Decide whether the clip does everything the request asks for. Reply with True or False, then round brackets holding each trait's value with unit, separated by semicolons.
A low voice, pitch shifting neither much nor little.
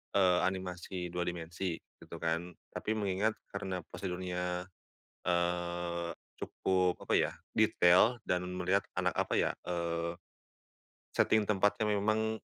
False (90 Hz; 2.0 semitones)